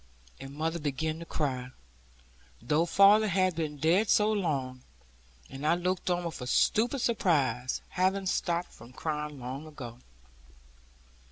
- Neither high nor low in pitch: Yes, medium, 160 Hz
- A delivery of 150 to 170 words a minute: No, average, 140 wpm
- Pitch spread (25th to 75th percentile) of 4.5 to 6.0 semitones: Yes, average, 5.2 semitones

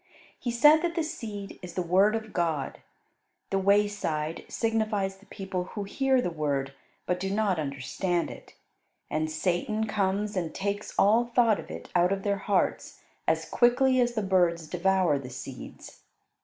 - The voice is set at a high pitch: Yes, high, 195 Hz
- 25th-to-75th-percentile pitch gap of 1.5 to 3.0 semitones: No, average, 4.0 semitones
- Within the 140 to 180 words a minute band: Yes, average, 165 wpm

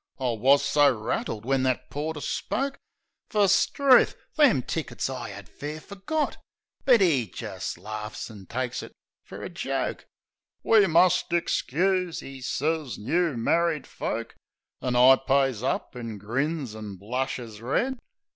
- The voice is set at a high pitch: No, low, 135 Hz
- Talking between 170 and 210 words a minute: No, average, 140 wpm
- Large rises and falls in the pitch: Yes, wide, 6.4 semitones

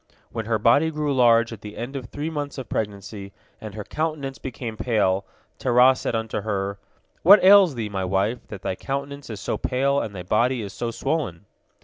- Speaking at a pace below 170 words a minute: No, average, 195 wpm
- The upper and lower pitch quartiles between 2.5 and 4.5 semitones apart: No, average, 5.0 semitones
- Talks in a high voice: No, low, 115 Hz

